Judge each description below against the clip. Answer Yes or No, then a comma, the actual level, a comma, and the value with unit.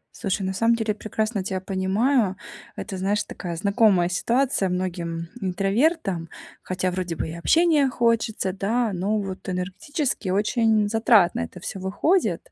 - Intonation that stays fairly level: No, average, 3.6 semitones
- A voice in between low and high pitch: No, high, 200 Hz